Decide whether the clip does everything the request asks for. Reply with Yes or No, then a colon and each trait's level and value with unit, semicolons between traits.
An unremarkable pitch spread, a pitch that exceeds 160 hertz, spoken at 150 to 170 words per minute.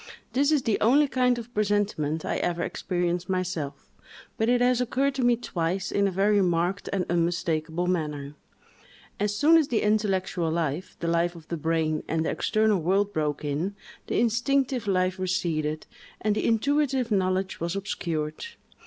Yes: average, 5.0 semitones; medium, 185 Hz; average, 165 wpm